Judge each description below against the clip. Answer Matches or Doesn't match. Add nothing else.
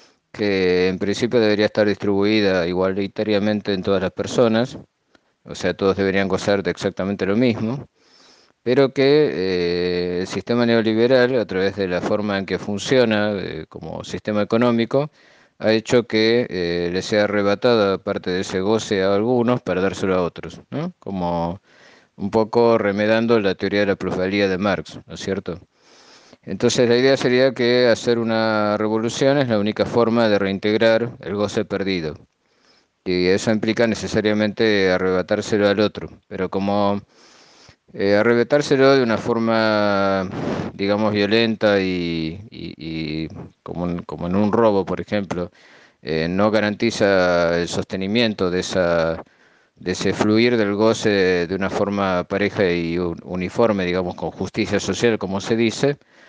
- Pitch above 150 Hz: Doesn't match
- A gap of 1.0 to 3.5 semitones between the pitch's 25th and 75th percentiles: Matches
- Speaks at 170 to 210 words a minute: Doesn't match